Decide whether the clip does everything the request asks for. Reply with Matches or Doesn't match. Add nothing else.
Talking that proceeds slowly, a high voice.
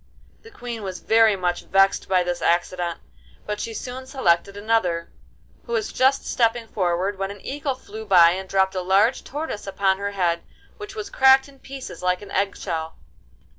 Doesn't match